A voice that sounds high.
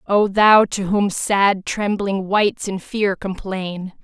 Yes: high, 195 Hz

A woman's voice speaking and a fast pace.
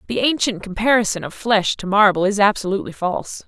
No: female; average, 175 wpm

